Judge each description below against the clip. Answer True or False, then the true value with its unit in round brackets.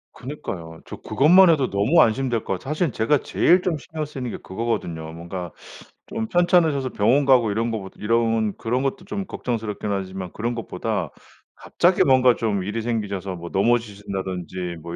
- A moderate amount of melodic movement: False (5.9 semitones)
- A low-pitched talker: True (115 Hz)